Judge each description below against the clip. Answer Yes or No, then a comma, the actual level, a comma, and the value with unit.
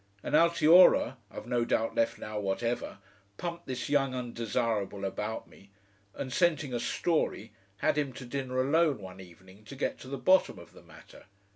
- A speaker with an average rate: Yes, average, 170 wpm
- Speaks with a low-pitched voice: Yes, low, 125 Hz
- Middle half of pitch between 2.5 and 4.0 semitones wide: No, average, 5.2 semitones